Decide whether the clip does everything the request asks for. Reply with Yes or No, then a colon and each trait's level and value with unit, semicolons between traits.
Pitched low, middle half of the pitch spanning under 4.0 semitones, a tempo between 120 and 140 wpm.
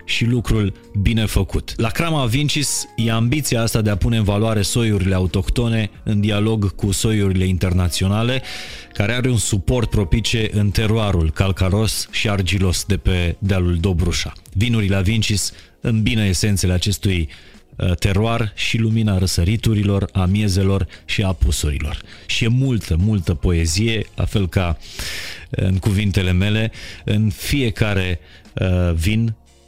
Yes: low, 100 Hz; average, 3.2 semitones; average, 135 wpm